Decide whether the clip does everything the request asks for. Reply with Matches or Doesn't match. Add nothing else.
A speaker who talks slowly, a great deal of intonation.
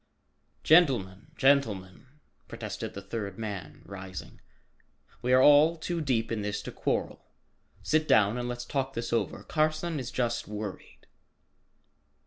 Matches